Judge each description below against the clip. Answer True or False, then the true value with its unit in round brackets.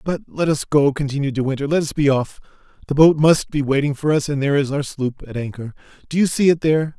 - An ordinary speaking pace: False (250 wpm)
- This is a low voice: False (145 Hz)